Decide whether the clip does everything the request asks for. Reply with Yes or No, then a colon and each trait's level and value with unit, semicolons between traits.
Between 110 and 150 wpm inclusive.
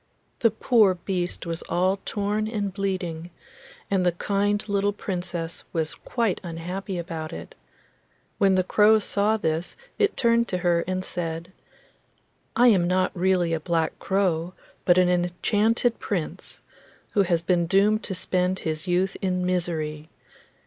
Yes: average, 145 wpm